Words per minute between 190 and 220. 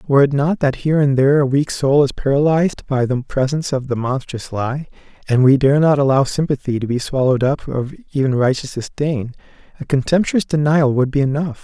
Yes: average, 200 wpm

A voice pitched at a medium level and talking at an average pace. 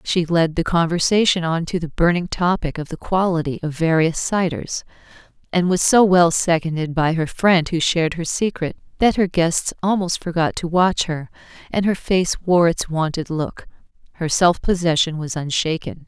Yes: medium, 170 Hz; average, 175 wpm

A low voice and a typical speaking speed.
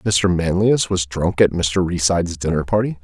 Yes: very low, 90 Hz; average, 180 wpm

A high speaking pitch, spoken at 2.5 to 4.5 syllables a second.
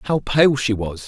No: low, 125 Hz; 4.0 syllables/s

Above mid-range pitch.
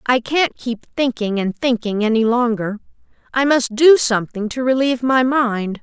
Yes: high, 240 Hz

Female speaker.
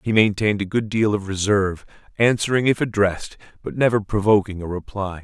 No: male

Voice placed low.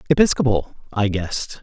Yes: low, 115 Hz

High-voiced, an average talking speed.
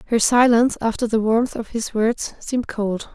Yes: high, 225 Hz; average, 190 wpm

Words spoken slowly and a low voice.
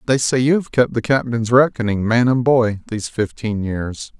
No: average, 200 wpm; low, 120 Hz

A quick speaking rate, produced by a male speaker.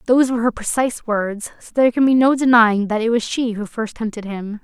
No: fast, 245 wpm; female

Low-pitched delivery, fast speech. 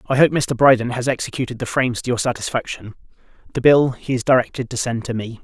Yes: low, 125 Hz; fast, 220 wpm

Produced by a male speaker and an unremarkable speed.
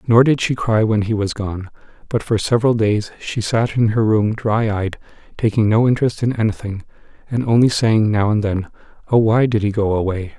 No: male; fast, 210 wpm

